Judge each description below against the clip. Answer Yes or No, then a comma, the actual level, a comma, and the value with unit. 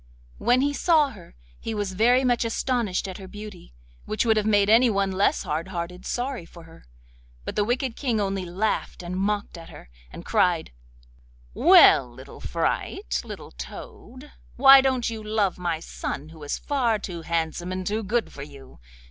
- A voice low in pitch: No, high, 205 Hz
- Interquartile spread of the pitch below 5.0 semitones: No, wide, 5.4 semitones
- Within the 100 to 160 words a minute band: No, average, 175 wpm